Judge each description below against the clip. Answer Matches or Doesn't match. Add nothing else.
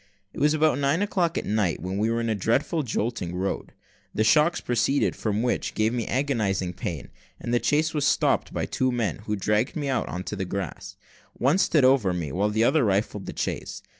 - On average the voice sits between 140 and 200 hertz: Doesn't match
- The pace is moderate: Doesn't match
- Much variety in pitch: Matches